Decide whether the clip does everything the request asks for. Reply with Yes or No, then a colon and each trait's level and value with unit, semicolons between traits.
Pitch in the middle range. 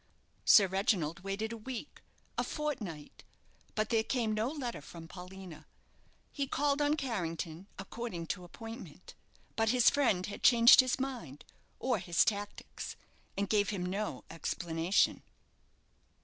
No: high, 210 Hz